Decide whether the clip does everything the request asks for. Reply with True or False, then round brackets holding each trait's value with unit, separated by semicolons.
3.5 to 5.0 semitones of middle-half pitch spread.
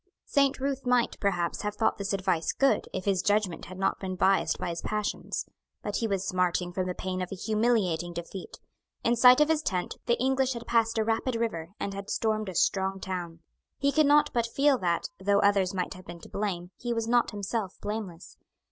True (4.2 semitones)